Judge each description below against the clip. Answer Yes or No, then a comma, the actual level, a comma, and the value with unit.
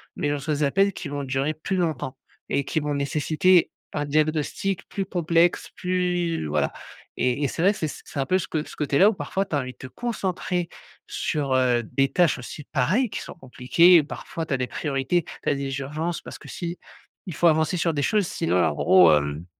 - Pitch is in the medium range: Yes, medium, 155 Hz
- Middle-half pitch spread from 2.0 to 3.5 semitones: No, average, 4.4 semitones